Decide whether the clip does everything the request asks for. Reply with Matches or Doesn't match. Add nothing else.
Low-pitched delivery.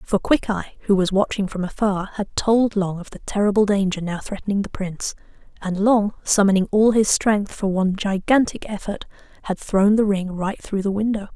Doesn't match